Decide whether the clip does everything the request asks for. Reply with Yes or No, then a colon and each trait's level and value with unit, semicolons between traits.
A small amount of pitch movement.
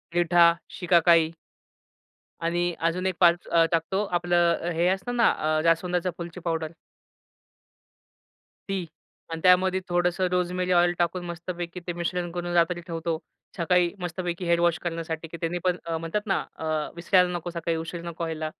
Yes: narrow, 1.2 semitones